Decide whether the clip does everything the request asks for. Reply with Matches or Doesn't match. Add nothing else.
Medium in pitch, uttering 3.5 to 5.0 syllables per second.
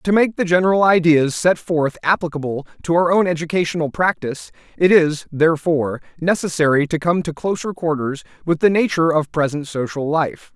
Doesn't match